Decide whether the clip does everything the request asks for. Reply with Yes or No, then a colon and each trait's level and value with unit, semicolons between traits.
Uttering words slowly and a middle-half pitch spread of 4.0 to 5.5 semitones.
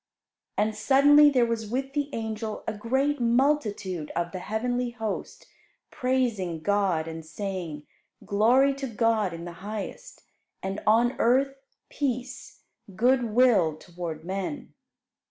Yes: slow, 125 wpm; average, 5.2 semitones